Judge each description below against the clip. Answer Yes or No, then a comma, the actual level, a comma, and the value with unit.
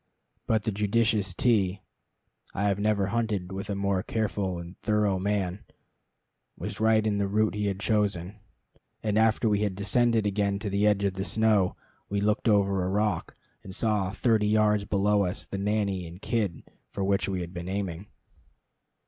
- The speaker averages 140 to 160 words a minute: No, average, 175 wpm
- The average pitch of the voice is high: No, low, 100 Hz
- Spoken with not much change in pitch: Yes, narrow, 1.7 semitones